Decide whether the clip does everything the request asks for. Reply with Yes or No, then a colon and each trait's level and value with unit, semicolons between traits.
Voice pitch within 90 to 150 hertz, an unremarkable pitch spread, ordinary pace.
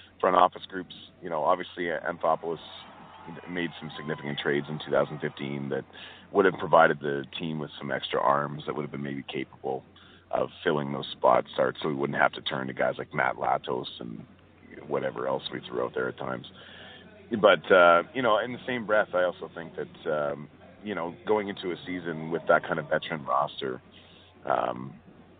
No: very low, 75 Hz; average, 3.6 semitones; average, 190 wpm